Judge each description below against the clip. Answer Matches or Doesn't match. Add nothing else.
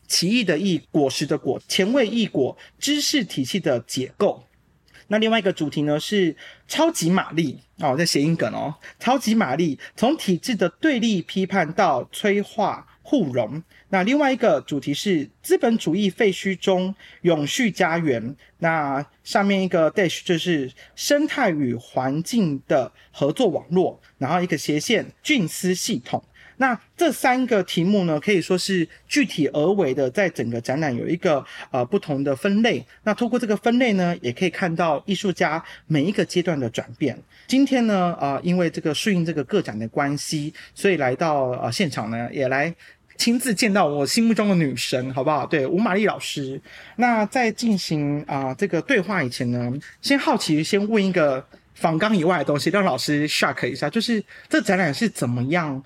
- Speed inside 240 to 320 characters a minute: Matches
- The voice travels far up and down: Matches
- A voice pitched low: Doesn't match